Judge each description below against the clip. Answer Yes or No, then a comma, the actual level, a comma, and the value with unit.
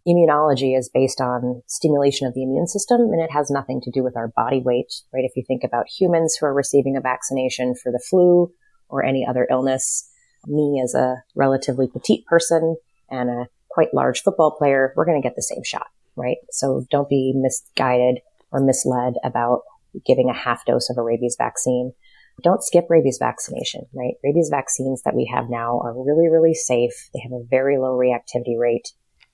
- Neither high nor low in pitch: No, low, 130 Hz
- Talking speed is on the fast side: No, average, 190 wpm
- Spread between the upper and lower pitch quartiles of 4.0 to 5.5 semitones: No, average, 3.1 semitones